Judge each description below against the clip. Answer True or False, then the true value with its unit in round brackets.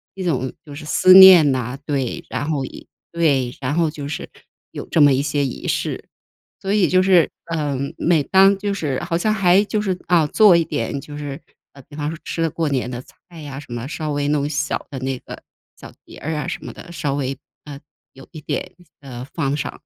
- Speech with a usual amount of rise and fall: True (3.9 semitones)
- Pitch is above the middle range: False (150 Hz)